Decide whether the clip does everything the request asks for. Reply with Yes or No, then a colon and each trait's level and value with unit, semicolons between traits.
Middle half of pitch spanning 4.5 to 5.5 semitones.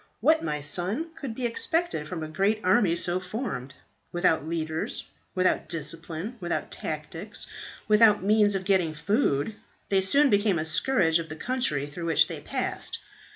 Yes: average, 5.2 semitones